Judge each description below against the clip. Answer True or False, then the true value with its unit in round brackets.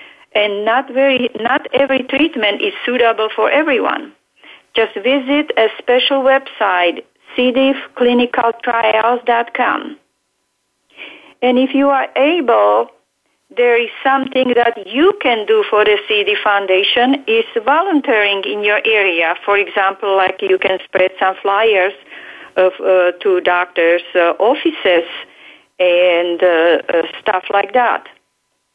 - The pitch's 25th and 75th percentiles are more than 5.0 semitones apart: True (5.5 semitones)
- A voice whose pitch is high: True (225 Hz)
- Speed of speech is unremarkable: False (120 wpm)